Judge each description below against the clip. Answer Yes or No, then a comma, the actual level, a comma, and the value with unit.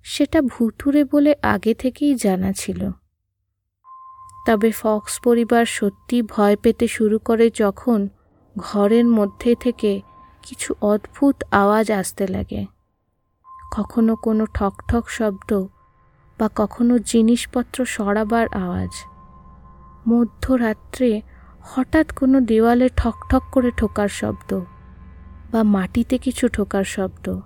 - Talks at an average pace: Yes, average, 100 wpm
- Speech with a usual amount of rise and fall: Yes, average, 3.8 semitones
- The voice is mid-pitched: No, high, 220 Hz